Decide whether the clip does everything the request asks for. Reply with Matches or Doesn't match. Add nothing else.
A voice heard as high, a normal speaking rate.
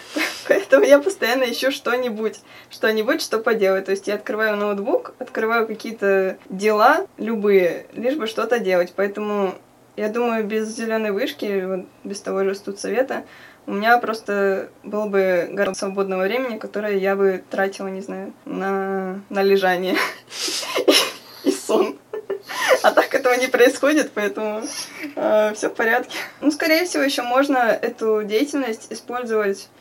Matches